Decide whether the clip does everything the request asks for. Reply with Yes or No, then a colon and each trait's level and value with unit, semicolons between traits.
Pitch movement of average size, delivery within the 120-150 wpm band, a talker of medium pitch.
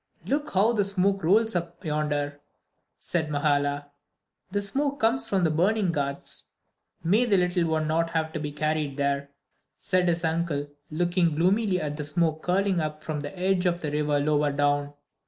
No: average, 4.1 semitones; average, 175 wpm; medium, 165 Hz